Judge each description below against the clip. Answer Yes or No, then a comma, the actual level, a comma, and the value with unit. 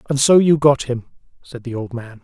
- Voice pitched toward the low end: Yes, low, 130 Hz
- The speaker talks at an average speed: No, fast, 240 wpm